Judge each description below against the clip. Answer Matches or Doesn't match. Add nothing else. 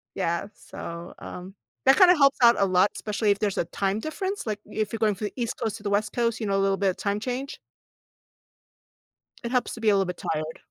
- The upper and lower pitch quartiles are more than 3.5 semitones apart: Doesn't match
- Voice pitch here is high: Matches